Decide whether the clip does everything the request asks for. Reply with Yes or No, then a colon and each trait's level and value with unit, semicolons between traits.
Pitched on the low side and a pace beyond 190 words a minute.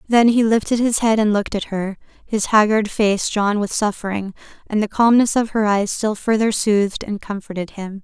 No: high, 210 Hz; average, 200 wpm